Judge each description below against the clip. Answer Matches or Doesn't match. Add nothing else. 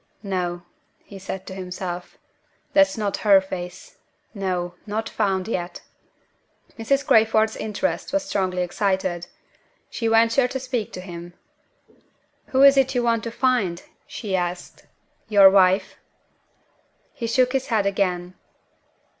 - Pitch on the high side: Matches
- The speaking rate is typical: Doesn't match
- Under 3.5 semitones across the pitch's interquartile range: Doesn't match